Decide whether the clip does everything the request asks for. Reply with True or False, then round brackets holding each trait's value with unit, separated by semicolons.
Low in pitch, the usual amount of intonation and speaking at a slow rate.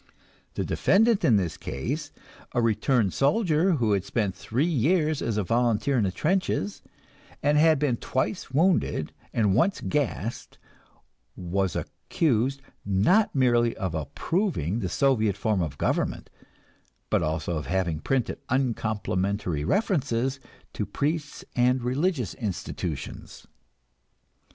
False (120 Hz; 6.9 semitones; 120 wpm)